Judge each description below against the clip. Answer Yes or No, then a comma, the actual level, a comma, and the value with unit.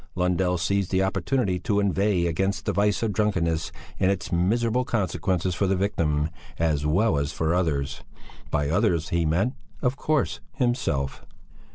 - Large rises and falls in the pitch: No, average, 3.9 semitones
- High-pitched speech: No, very low, 90 Hz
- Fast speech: No, average, 155 wpm